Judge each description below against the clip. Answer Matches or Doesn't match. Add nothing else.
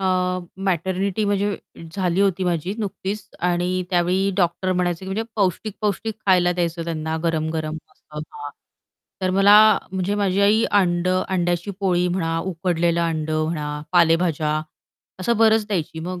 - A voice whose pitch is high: Doesn't match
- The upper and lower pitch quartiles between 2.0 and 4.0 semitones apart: Matches